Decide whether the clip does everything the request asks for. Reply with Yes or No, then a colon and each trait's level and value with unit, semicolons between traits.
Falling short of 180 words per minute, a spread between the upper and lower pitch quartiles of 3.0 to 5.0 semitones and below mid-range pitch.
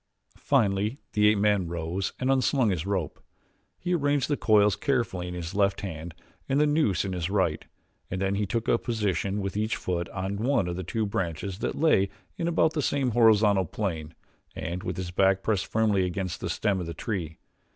No: average, 200 wpm; average, 3.8 semitones; low, 100 Hz